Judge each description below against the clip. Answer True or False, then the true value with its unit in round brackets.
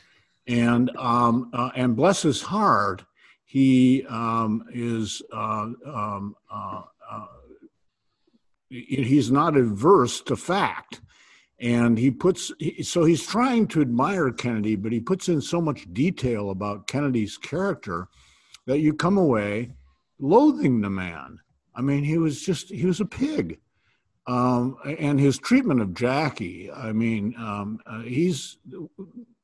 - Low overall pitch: True (125 Hz)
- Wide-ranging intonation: True (5.7 semitones)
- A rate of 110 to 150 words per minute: True (135 wpm)